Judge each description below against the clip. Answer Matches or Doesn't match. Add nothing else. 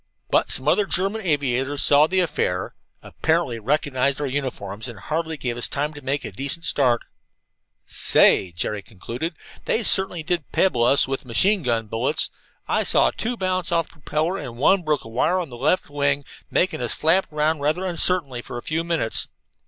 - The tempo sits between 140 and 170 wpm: Doesn't match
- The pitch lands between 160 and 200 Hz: Doesn't match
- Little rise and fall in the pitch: Doesn't match